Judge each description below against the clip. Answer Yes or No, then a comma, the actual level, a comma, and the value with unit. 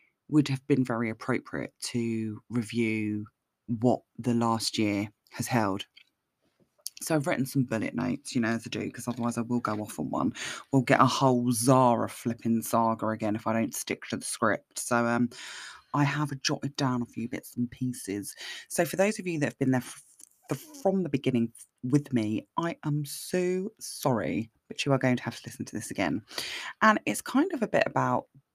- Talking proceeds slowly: No, fast, 205 wpm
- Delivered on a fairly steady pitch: No, average, 3.4 semitones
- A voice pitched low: Yes, low, 120 Hz